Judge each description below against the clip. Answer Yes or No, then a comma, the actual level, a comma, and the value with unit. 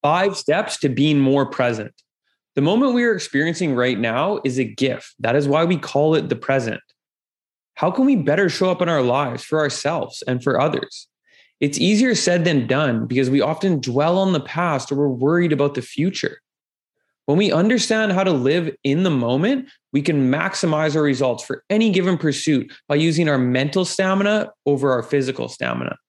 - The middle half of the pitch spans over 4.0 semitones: Yes, wide, 5.5 semitones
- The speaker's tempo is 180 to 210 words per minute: Yes, average, 190 wpm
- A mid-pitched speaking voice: Yes, medium, 150 Hz